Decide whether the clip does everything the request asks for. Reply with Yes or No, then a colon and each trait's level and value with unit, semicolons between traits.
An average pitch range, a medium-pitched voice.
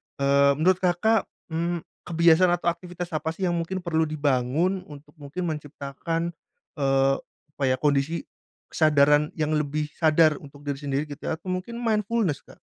Yes: average, 3.5 semitones; medium, 160 Hz